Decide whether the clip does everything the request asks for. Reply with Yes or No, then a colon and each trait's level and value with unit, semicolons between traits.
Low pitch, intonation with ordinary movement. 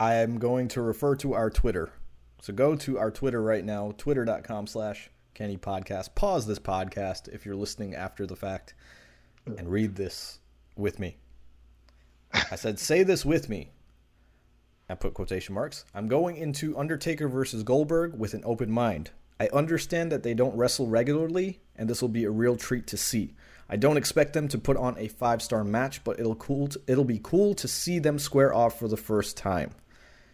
No: low, 110 Hz; wide, 5.7 semitones